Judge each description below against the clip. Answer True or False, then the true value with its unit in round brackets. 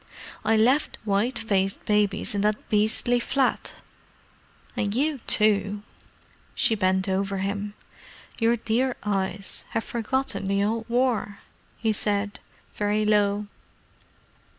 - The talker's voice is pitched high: True (210 Hz)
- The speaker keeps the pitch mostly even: True (2.2 semitones)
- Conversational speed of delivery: False (115 wpm)